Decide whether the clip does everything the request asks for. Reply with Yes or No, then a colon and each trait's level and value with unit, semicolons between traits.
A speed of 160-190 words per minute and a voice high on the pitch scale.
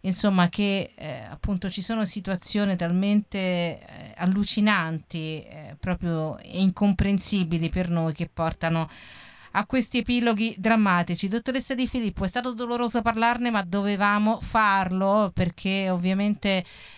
No: slow, 115 wpm; high, 195 Hz